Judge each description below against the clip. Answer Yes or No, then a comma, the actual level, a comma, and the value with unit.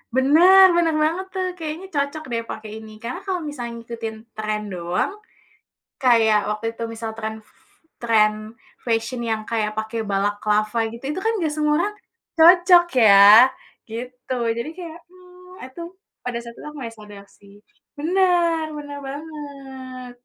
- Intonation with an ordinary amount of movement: No, wide, 6.5 semitones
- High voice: Yes, very high, 255 Hz